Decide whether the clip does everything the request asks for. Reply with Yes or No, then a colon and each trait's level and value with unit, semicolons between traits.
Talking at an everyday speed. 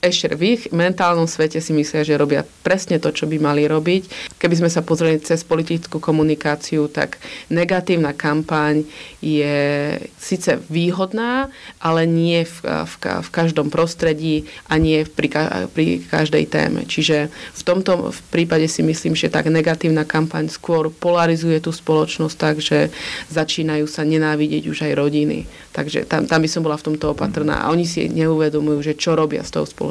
No: fast, 170 wpm